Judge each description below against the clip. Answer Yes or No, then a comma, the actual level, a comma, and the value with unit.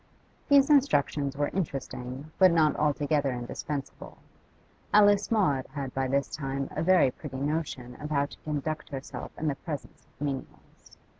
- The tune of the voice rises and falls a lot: No, average, 3.0 semitones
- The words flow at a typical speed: Yes, average, 150 wpm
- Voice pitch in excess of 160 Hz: No, medium, 145 Hz